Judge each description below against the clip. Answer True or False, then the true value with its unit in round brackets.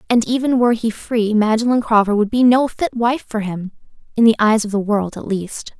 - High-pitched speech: True (225 Hz)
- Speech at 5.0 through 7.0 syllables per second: True (5.3 syllables/s)